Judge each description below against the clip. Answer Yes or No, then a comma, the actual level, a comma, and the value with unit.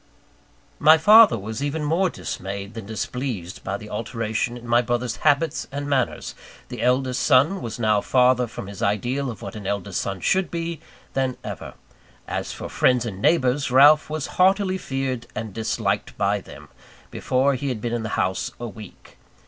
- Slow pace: No, average, 175 wpm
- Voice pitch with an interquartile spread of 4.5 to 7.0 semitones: Yes, average, 4.8 semitones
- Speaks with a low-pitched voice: Yes, low, 125 Hz